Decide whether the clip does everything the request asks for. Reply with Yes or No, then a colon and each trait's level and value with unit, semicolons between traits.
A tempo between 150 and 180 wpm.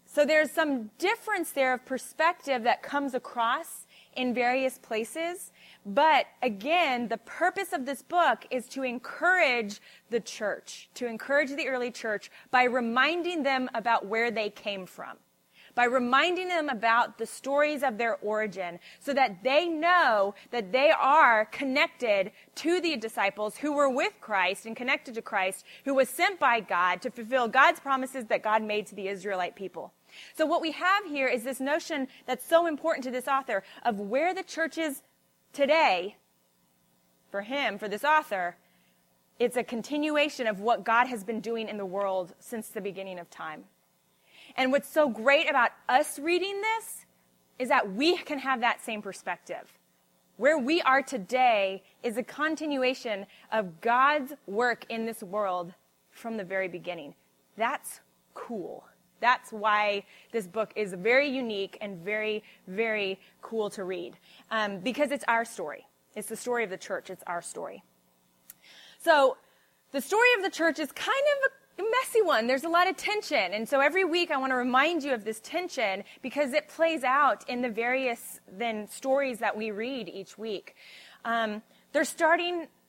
Yes: average, 170 wpm